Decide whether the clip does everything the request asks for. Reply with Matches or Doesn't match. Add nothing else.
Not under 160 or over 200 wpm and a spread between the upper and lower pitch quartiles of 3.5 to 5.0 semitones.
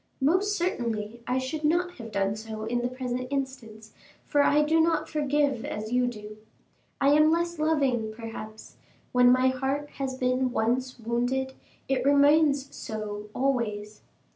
Doesn't match